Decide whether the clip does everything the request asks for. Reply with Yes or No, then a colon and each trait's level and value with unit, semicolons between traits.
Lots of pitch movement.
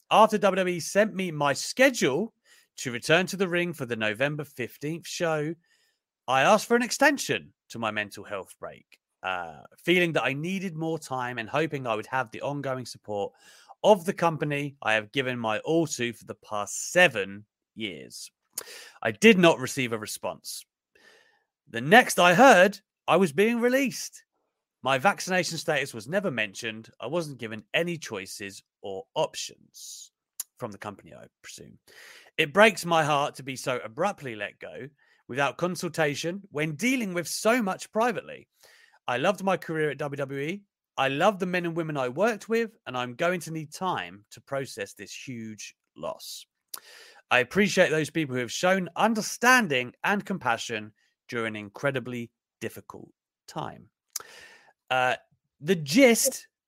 Yes: wide, 8.0 semitones